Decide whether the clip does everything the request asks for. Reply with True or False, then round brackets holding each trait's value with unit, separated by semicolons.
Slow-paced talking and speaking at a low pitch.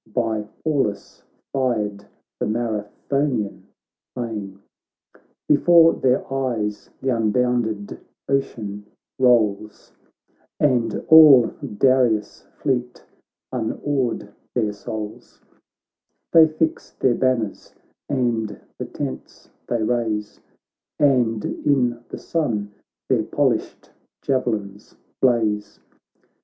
True (85 wpm; 120 Hz)